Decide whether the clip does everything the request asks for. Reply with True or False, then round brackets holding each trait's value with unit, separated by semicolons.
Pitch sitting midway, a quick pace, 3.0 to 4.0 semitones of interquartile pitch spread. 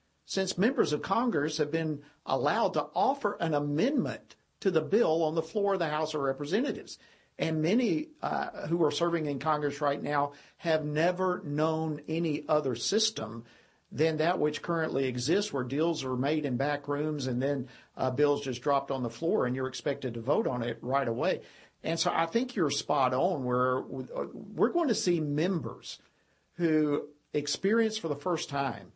False (150 Hz; 180 wpm; 3.4 semitones)